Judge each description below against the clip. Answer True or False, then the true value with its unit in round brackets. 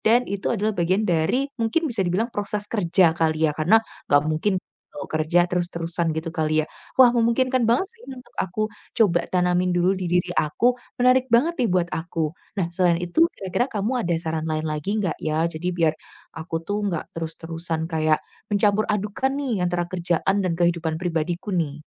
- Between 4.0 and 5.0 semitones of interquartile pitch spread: True (4.4 semitones)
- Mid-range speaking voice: True (175 Hz)